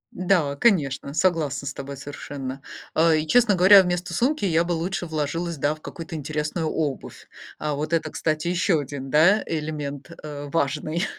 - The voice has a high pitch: No, medium, 155 Hz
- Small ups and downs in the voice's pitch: No, average, 3.3 semitones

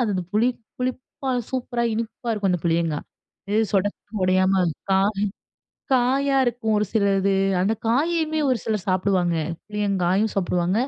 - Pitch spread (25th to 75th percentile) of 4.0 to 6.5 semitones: Yes, average, 4.3 semitones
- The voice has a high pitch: Yes, high, 210 Hz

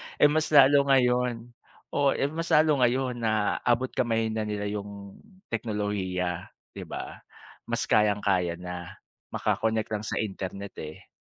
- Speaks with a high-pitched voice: No, low, 110 Hz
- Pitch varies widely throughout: No, average, 4.3 semitones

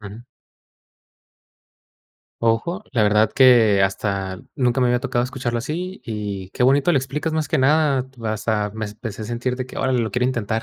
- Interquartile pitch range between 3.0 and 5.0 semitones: Yes, average, 3.6 semitones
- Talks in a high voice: No, low, 120 Hz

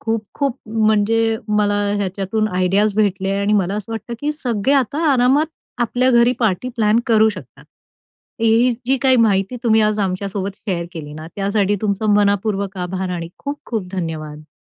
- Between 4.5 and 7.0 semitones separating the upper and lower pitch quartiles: No, average, 2.9 semitones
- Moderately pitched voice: No, high, 210 Hz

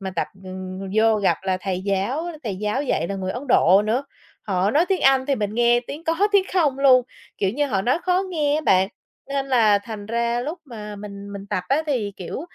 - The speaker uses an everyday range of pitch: No, wide, 5.7 semitones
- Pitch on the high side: Yes, high, 225 Hz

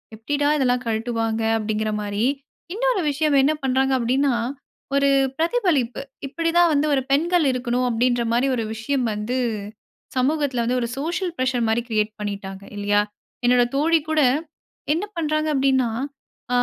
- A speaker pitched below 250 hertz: No, very high, 255 Hz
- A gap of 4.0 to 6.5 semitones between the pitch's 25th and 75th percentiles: Yes, average, 4.7 semitones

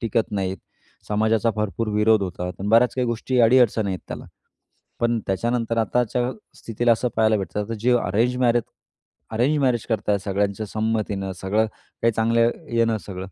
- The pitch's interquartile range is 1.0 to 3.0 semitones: Yes, narrow, 2.5 semitones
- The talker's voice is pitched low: Yes, low, 110 Hz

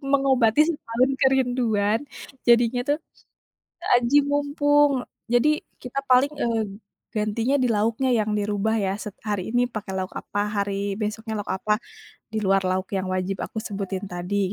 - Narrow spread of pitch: No, average, 3.8 semitones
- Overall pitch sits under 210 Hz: No, high, 220 Hz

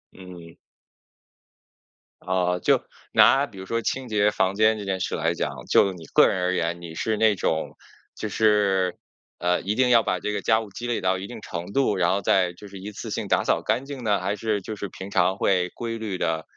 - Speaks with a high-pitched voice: No, low, 100 Hz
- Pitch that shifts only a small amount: No, average, 3.2 semitones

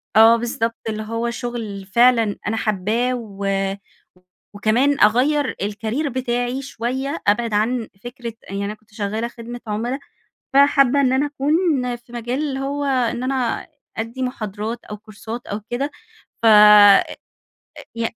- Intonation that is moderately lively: Yes, average, 3.1 semitones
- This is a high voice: Yes, high, 235 Hz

